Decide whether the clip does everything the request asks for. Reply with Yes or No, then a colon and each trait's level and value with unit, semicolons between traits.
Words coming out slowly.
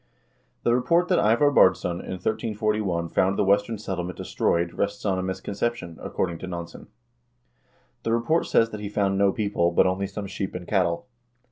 No: average, 170 wpm